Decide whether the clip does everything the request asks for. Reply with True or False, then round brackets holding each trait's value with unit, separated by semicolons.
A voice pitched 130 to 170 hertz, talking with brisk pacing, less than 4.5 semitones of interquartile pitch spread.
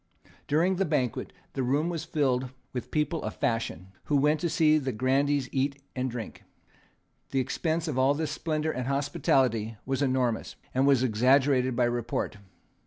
False (135 Hz; 165 wpm; 3.1 semitones)